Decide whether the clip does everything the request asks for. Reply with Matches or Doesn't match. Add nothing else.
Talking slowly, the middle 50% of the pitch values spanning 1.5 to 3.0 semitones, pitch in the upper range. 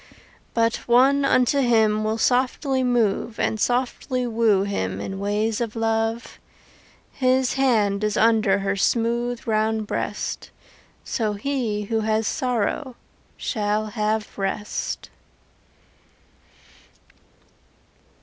Matches